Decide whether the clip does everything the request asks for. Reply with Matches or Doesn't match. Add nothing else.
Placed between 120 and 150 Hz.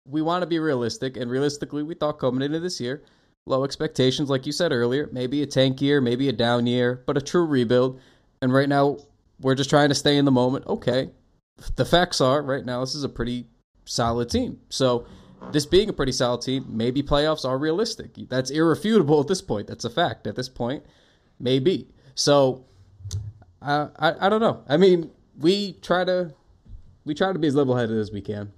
Matches